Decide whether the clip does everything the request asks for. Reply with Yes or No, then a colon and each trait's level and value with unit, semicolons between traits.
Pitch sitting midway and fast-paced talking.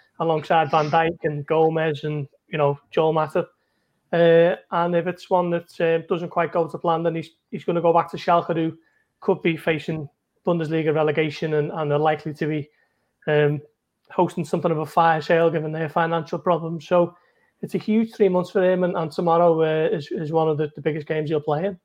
Yes: medium, 165 Hz; fast, 215 wpm